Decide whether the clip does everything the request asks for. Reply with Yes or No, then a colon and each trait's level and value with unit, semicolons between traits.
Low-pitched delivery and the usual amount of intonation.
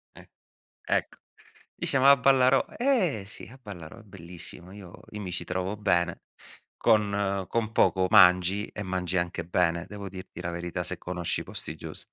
Yes: very low, 95 Hz; average, 3.4 semitones